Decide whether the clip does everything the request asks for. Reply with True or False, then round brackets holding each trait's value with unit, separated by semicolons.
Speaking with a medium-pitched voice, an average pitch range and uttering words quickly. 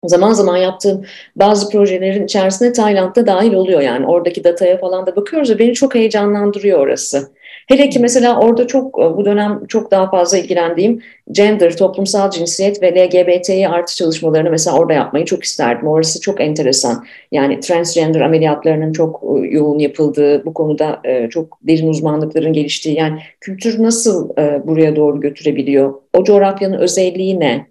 True (180 Hz; 4.4 semitones; 145 wpm)